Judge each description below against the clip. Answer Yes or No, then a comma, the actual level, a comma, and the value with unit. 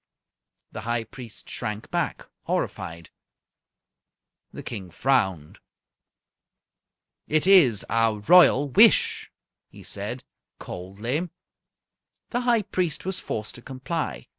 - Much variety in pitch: Yes, wide, 8.2 semitones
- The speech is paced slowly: Yes, slow, 100 wpm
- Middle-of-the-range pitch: No, low, 120 Hz